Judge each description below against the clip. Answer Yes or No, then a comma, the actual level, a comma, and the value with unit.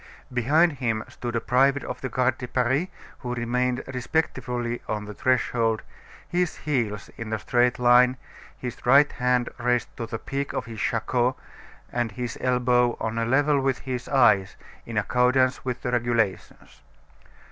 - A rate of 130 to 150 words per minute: No, average, 160 wpm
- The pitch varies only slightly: Yes, narrow, 1.7 semitones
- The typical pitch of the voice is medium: No, low, 125 Hz